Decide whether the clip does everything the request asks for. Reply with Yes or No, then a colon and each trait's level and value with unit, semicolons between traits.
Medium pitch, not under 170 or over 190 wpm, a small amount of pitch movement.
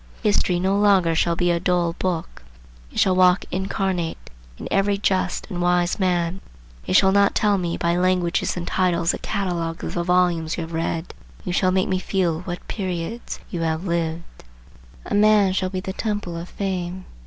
Yes: medium, 180 Hz; average, 185 wpm; narrow, 1.9 semitones